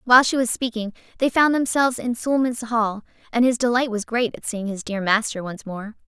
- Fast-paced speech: Yes, fast, 215 wpm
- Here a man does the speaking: No, female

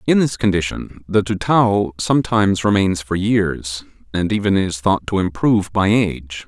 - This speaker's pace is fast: No, average, 160 wpm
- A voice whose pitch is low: Yes, low, 100 Hz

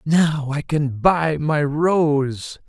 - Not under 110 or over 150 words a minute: Yes, slow, 135 wpm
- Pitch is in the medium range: Yes, medium, 150 Hz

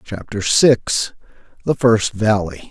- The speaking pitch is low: Yes, low, 110 Hz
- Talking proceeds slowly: Yes, slow, 110 wpm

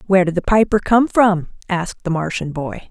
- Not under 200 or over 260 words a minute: Yes, fast, 205 wpm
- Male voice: No, female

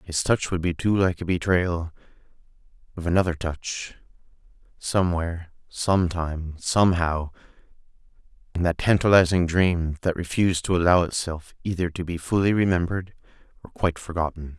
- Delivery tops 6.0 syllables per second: No, 5.4 syllables/s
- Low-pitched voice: Yes, very low, 85 Hz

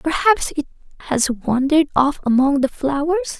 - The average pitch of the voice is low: No, very high, 275 Hz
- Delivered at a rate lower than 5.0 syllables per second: No, 5.2 syllables/s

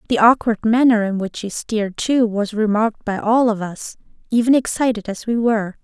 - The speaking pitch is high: Yes, high, 220 Hz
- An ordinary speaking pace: Yes, average, 195 wpm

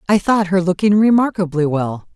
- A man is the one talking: No, female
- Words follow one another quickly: No, average, 165 wpm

